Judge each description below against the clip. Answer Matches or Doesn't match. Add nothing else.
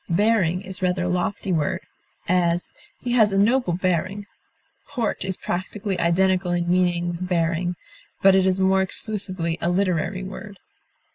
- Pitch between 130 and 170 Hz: Doesn't match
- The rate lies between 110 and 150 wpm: Matches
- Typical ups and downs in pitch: Doesn't match